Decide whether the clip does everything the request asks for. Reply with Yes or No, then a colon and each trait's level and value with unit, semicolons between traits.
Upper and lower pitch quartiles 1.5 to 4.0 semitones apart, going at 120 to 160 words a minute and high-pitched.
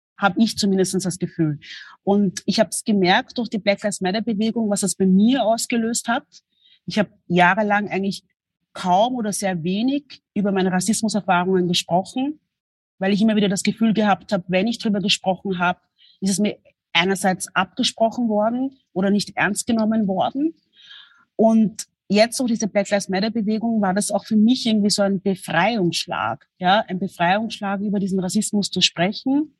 No: average, 2.9 semitones; average, 170 wpm; high, 205 Hz